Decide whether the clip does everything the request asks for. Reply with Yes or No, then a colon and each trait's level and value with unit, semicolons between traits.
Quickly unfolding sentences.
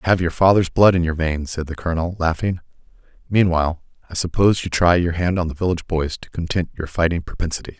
Yes: fast, 215 wpm